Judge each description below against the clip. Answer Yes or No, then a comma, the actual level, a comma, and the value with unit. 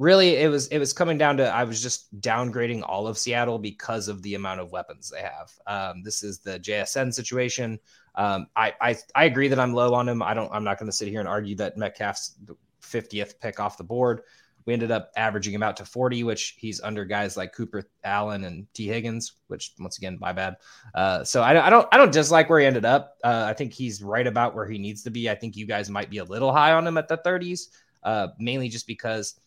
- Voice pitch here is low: Yes, low, 115 Hz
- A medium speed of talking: No, fast, 245 wpm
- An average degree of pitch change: Yes, average, 3.3 semitones